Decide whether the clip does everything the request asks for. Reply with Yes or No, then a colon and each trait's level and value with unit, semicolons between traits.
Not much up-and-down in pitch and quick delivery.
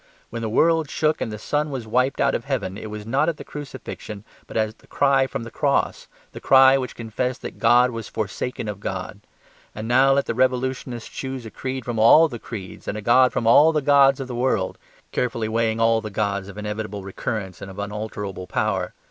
No: average, 3.7 semitones; fast, 215 wpm